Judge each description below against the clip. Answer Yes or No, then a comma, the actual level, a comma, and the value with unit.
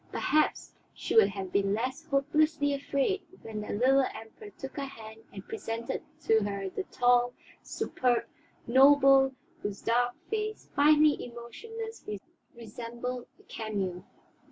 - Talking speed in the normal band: No, slow, 130 wpm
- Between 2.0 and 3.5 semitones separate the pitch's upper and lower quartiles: No, average, 4.4 semitones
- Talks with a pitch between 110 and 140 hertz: No, high, 245 Hz